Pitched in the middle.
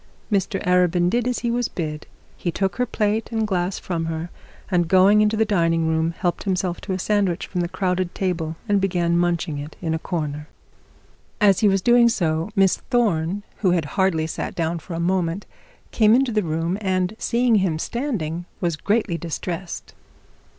Yes: medium, 180 Hz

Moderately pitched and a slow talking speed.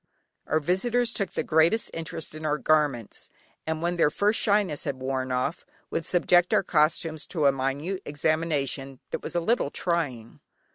No: medium, 155 Hz; average, 170 wpm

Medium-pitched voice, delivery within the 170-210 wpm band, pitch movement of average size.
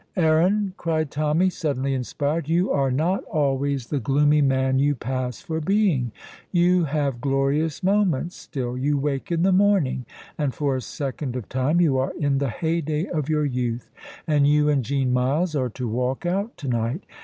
Yes: medium, 145 Hz; average, 180 wpm; average, 3.7 semitones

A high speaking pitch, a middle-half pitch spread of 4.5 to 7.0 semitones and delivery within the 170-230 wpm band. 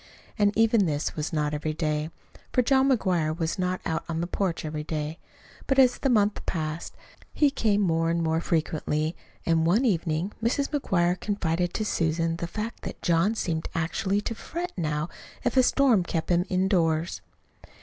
No: medium, 175 Hz; average, 4.8 semitones; average, 175 wpm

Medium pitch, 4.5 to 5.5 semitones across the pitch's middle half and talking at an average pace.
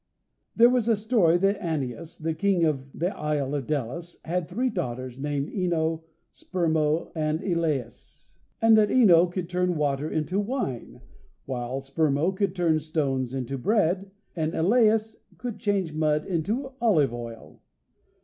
Yes: medium, 165 Hz; average, 5.2 semitones; average, 145 wpm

